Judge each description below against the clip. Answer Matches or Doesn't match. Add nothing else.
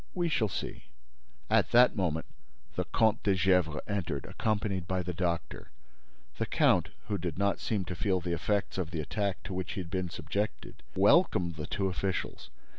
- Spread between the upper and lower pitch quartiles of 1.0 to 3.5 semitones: Matches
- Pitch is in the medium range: Doesn't match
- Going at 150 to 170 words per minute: Doesn't match